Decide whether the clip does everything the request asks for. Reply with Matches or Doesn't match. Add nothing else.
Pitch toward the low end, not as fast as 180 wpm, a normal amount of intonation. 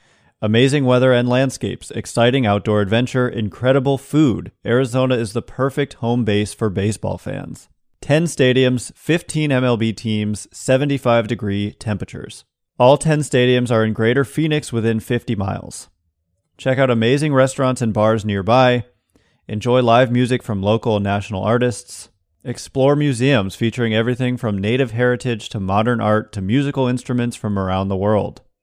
Matches